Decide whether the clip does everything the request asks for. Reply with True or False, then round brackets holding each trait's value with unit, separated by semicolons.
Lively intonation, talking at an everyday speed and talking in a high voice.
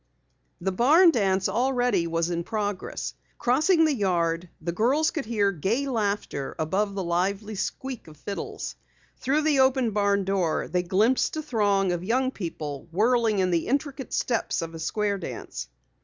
True (6.0 semitones; 160 wpm; 205 Hz)